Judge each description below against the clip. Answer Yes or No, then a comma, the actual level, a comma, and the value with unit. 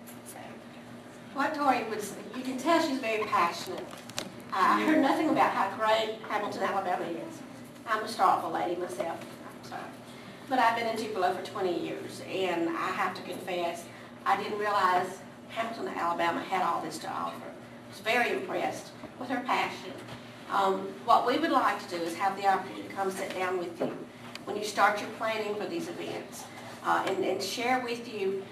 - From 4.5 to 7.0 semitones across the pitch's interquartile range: No, average, 3.6 semitones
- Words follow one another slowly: No, average, 185 wpm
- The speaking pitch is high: Yes, high, 205 Hz